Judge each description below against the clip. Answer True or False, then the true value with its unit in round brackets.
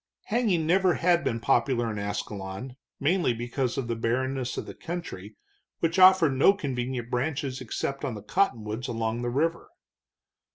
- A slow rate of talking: False (155 wpm)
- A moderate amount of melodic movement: False (6.0 semitones)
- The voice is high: False (130 Hz)